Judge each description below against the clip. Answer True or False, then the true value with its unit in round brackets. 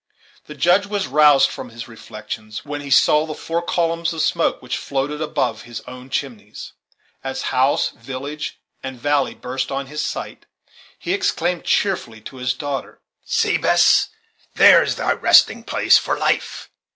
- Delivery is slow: False (160 wpm)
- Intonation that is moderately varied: True (3.8 semitones)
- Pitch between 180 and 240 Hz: False (140 Hz)